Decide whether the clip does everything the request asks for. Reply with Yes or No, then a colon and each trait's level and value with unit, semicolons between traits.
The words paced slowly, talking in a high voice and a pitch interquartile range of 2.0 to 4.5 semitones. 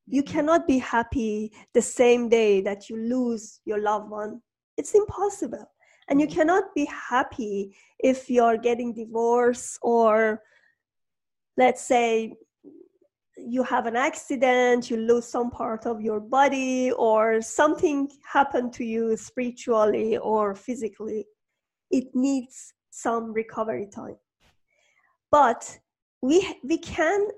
Yes: slow, 120 wpm; high, 245 Hz; average, 3.8 semitones